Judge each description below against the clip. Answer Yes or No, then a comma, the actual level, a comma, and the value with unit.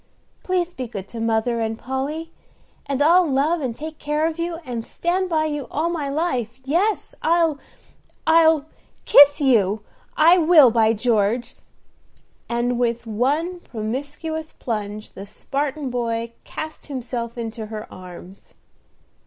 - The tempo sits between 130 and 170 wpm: Yes, slow, 135 wpm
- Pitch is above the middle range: Yes, very high, 265 Hz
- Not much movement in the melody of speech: No, wide, 5.6 semitones